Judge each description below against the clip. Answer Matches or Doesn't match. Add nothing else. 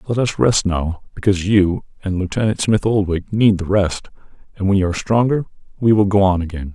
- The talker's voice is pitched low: Matches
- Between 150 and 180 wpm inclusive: Doesn't match